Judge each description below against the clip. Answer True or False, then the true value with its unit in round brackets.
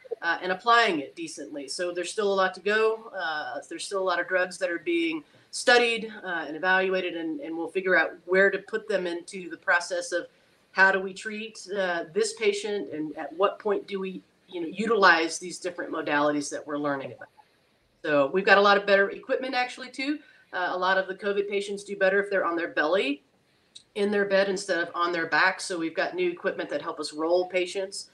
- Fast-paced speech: True (220 wpm)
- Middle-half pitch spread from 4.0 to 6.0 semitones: False (3.2 semitones)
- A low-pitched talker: False (190 Hz)